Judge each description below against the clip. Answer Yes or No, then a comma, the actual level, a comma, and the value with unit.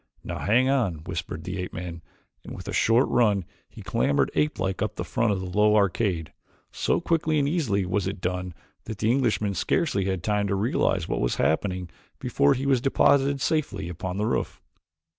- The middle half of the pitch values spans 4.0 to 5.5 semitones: Yes, average, 5.1 semitones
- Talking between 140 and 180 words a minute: No, average, 190 wpm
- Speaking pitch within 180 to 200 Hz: No, low, 100 Hz